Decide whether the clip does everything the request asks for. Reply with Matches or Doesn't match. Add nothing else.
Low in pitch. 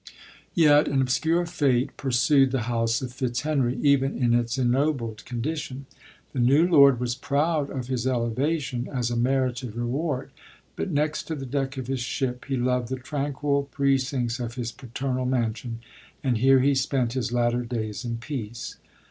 Matches